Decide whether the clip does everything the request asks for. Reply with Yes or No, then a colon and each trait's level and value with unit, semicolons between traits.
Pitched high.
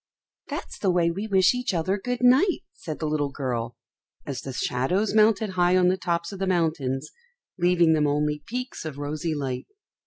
No: medium, 170 Hz